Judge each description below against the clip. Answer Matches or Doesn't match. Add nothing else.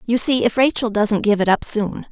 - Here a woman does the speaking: Matches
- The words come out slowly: Doesn't match